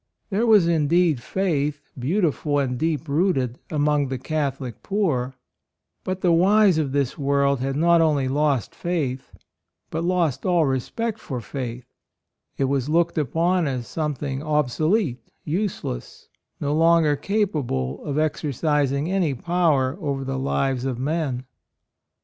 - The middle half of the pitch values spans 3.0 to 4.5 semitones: Yes, average, 4.1 semitones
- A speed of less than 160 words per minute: Yes, average, 140 wpm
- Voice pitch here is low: No, medium, 150 Hz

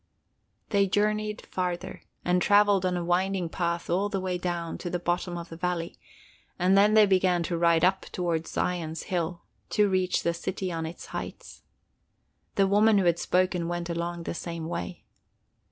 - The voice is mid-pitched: Yes, medium, 180 Hz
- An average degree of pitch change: No, narrow, 2.0 semitones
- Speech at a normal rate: Yes, average, 175 wpm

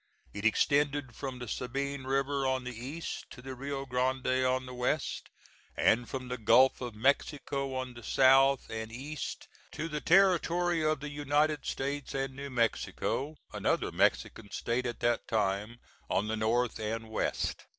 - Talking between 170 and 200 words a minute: No, average, 160 wpm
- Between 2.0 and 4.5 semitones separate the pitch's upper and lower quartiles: Yes, average, 2.9 semitones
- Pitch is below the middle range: Yes, low, 130 Hz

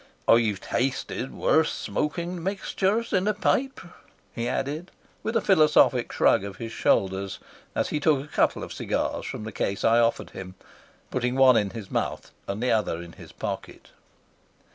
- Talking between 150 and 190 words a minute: Yes, average, 165 wpm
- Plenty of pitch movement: Yes, wide, 7.8 semitones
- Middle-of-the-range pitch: No, low, 130 Hz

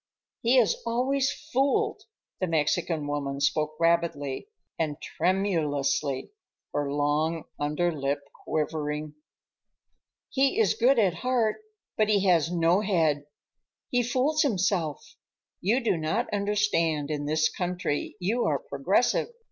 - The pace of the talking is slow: Yes, slow, 115 wpm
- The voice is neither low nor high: Yes, medium, 170 Hz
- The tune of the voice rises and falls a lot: Yes, wide, 6.4 semitones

